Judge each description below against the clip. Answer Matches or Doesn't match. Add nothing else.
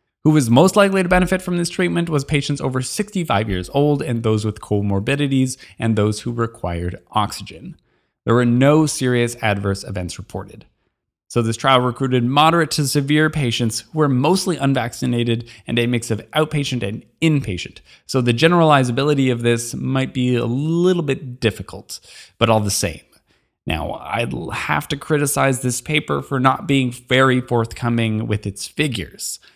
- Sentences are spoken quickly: Doesn't match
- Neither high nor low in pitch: Doesn't match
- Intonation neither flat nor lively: Matches